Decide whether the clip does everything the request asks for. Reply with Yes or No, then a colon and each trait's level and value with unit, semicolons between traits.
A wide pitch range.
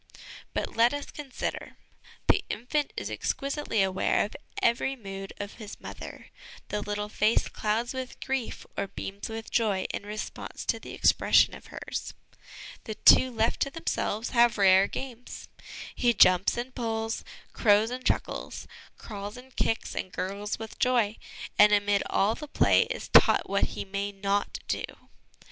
No: average, 3.2 semitones